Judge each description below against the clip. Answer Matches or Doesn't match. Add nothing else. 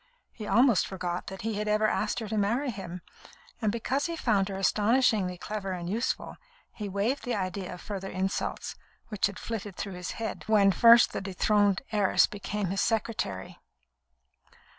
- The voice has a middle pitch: Doesn't match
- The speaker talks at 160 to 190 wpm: Matches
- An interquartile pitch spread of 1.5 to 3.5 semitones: Matches